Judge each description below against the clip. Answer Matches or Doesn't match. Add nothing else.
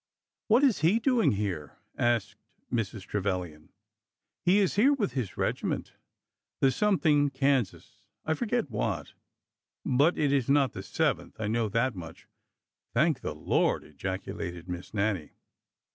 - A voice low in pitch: Matches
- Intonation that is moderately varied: Doesn't match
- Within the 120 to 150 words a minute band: Matches